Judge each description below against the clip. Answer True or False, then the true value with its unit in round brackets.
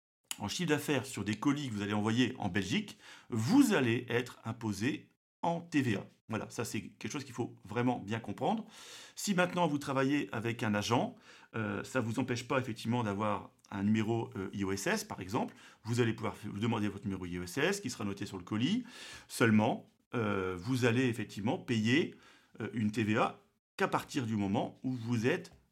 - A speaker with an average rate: True (185 wpm)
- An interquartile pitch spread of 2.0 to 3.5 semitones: False (3.9 semitones)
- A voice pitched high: False (115 Hz)